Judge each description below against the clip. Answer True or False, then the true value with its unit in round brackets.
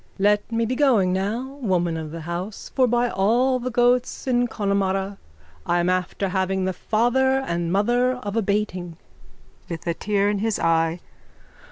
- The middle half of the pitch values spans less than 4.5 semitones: False (4.8 semitones)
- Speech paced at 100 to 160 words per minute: False (170 wpm)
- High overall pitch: True (205 Hz)